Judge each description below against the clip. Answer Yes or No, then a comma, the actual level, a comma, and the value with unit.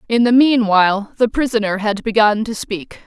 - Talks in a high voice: Yes, high, 220 Hz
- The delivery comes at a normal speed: Yes, average, 175 wpm